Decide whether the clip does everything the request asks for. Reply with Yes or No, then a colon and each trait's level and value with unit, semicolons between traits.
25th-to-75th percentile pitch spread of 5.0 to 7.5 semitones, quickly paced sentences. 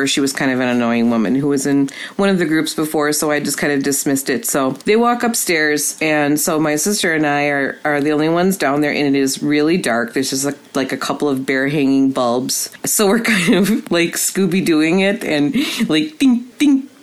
Yes: wide, 5.5 semitones; fast, 235 wpm